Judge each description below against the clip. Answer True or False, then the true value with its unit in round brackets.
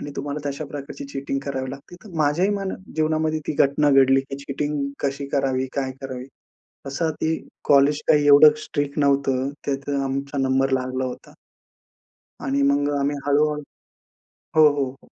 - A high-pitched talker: False (140 Hz)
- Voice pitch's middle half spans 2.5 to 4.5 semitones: False (1.4 semitones)